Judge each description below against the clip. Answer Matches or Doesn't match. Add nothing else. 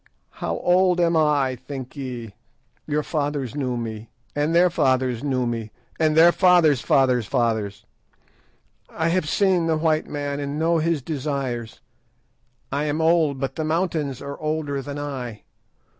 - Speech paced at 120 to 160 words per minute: Matches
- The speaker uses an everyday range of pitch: Matches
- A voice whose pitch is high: Doesn't match